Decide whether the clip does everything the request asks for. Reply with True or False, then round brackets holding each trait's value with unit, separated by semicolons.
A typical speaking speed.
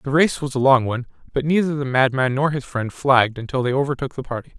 False (250 wpm)